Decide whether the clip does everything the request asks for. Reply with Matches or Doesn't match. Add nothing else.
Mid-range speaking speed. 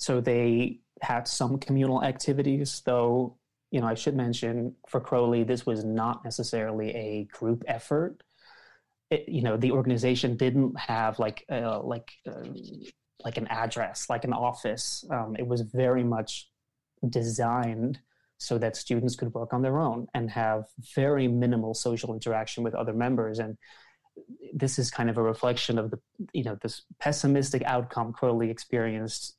Matches